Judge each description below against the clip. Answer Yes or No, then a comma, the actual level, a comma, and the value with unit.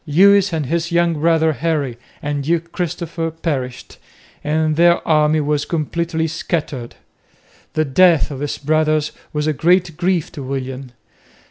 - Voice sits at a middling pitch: Yes, medium, 155 Hz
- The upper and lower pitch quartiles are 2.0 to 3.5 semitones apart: Yes, narrow, 2.4 semitones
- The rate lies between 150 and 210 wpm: No, average, 140 wpm